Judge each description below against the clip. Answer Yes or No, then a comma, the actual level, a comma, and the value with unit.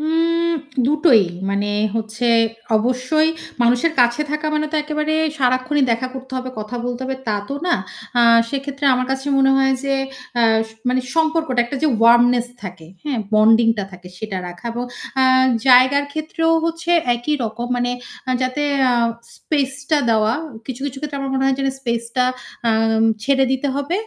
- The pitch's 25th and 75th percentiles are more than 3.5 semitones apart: Yes, average, 3.9 semitones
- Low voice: No, very high, 260 Hz